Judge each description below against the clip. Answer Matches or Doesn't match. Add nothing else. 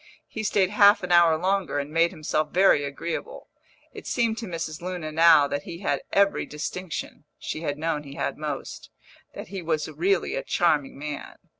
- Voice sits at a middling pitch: Matches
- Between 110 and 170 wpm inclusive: Doesn't match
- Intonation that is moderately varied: Matches